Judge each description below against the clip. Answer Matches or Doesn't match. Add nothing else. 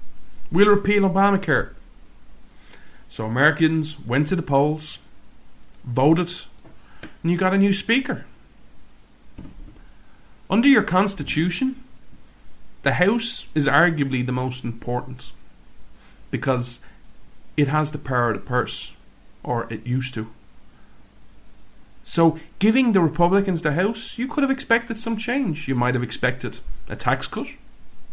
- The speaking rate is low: Matches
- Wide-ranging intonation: Matches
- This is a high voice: Doesn't match